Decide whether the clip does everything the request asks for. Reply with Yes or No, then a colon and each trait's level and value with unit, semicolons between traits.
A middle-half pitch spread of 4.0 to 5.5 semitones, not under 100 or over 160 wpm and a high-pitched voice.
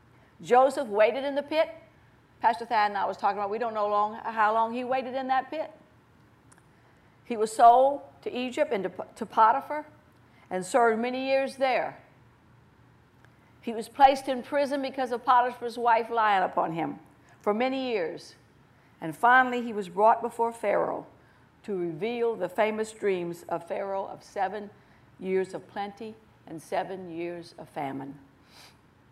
Yes: average, 4.6 semitones; average, 155 wpm; high, 225 Hz